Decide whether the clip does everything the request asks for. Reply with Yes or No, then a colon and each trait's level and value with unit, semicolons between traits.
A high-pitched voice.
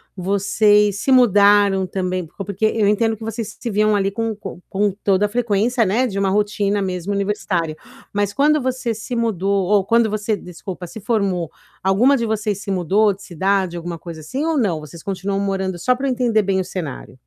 Yes: high, 200 Hz